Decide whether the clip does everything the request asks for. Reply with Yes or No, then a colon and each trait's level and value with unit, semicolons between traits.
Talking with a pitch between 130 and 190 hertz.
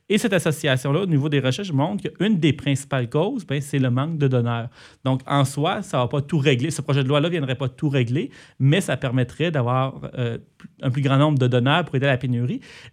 Yes: medium, 140 Hz